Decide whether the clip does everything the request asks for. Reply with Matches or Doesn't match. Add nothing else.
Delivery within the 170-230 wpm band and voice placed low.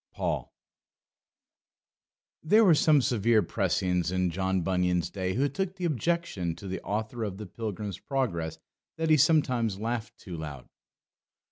Doesn't match